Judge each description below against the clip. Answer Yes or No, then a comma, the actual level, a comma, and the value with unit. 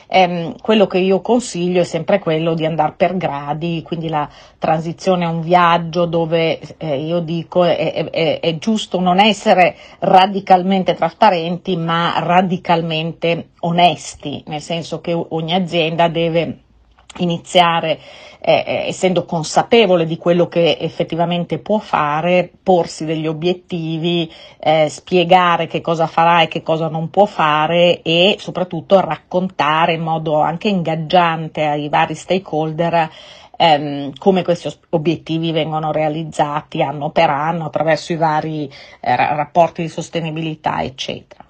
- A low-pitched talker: No, medium, 170 Hz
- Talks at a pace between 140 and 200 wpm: No, average, 125 wpm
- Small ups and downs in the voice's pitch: Yes, narrow, 2.0 semitones